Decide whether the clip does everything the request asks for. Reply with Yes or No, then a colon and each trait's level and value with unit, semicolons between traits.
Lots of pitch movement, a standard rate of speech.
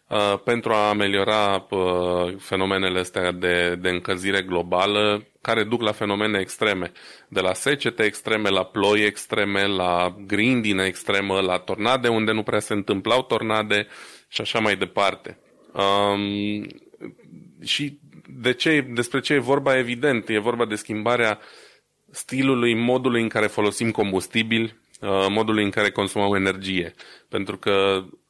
No: average, 2.9 semitones; average, 130 wpm